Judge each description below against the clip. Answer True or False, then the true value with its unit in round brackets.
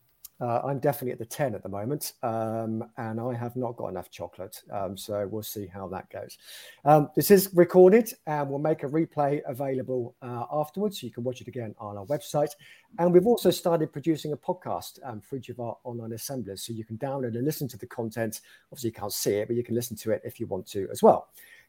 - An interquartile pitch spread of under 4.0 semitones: False (4.7 semitones)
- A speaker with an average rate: False (235 wpm)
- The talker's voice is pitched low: True (125 Hz)